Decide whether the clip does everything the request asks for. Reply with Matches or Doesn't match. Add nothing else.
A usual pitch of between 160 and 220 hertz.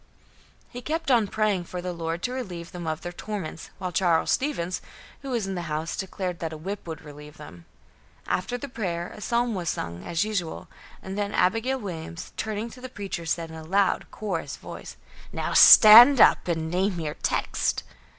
Matches